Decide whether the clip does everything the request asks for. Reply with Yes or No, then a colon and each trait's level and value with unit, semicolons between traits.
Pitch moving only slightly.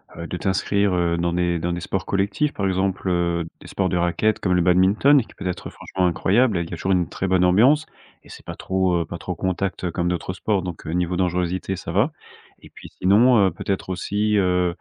Yes: narrow, 2.0 semitones